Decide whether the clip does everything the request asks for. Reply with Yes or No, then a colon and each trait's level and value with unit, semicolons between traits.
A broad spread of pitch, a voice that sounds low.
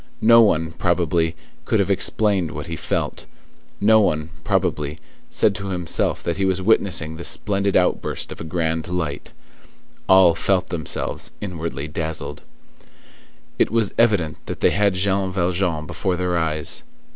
No: average, 3.4 semitones; very low, 90 Hz